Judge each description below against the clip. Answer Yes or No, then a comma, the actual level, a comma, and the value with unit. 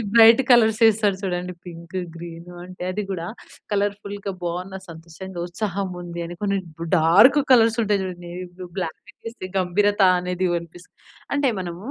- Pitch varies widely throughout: No, average, 2.9 semitones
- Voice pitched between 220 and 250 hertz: No, medium, 185 Hz